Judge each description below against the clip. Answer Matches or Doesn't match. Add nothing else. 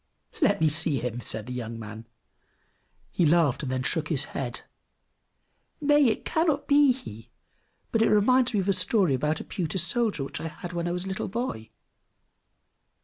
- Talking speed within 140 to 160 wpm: Doesn't match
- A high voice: Doesn't match